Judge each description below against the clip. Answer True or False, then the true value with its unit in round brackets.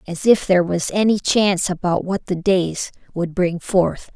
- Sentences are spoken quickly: False (190 wpm)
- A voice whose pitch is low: False (185 Hz)